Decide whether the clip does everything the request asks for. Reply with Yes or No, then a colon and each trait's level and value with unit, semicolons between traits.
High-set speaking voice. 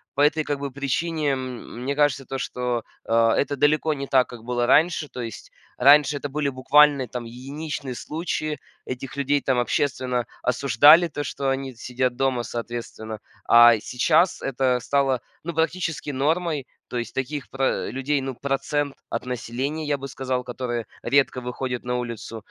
No: low, 135 Hz